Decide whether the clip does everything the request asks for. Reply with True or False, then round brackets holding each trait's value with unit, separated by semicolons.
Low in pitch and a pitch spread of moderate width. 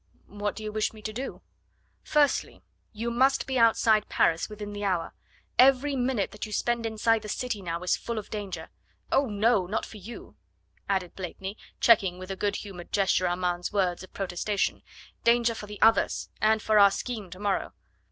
False (210 Hz; 3.1 semitones)